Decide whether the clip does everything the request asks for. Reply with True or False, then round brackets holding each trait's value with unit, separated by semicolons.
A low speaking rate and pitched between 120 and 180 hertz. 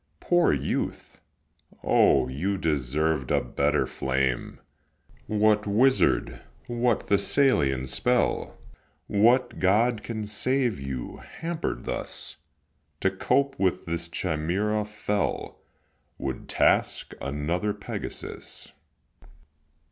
False (90 wpm; 100 Hz)